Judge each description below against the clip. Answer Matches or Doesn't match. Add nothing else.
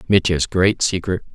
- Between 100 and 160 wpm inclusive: Matches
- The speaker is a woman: Doesn't match